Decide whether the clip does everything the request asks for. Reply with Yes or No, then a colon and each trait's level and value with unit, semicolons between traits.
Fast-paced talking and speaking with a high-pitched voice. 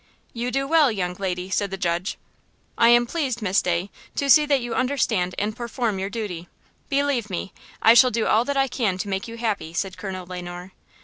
Yes: fast, 210 wpm; high, 215 Hz